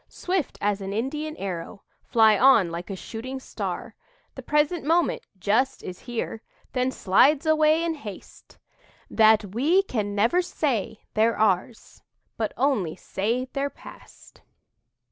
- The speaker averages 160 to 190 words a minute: No, slow, 135 wpm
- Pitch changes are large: Yes, wide, 6.4 semitones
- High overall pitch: Yes, high, 235 Hz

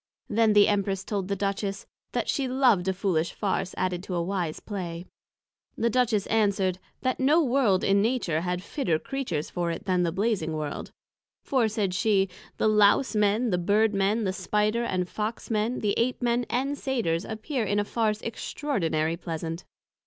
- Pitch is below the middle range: No, high, 205 Hz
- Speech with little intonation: No, average, 4.0 semitones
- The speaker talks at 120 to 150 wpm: No, average, 175 wpm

